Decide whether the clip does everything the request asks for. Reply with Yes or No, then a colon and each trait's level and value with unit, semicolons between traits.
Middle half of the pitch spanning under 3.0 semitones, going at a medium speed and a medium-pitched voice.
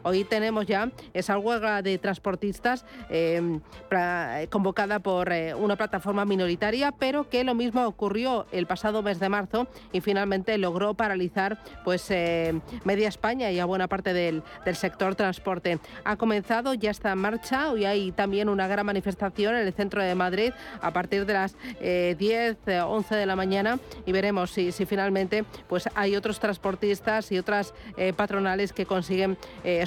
No: narrow, 2.5 semitones; average, 170 wpm; high, 200 Hz